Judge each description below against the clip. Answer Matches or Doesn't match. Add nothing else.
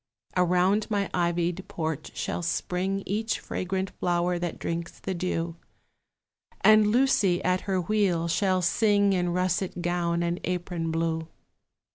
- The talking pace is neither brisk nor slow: Doesn't match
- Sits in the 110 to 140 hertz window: Doesn't match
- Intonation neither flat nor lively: Doesn't match